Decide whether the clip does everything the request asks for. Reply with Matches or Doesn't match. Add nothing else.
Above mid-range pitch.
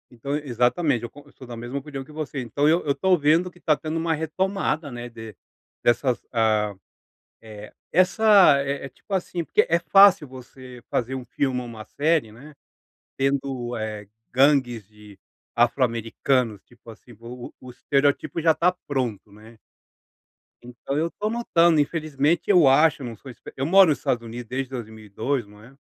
Doesn't match